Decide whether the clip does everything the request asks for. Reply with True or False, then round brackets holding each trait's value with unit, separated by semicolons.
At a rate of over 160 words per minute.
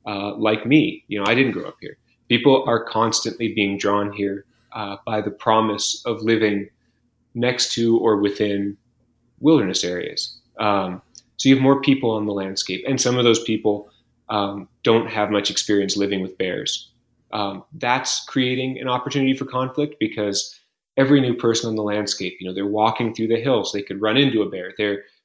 True (185 wpm)